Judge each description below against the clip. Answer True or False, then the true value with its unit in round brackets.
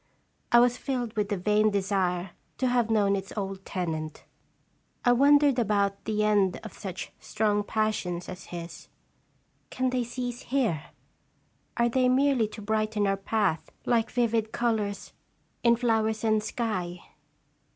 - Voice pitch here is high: True (215 Hz)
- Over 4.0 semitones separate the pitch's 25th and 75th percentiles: False (3.4 semitones)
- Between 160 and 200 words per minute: False (140 wpm)